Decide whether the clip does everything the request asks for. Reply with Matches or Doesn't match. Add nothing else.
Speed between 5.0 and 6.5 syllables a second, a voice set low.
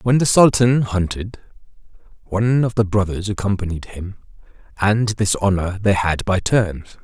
Doesn't match